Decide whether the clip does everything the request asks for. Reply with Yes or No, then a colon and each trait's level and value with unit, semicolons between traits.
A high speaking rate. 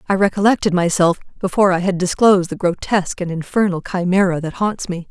No: average, 175 wpm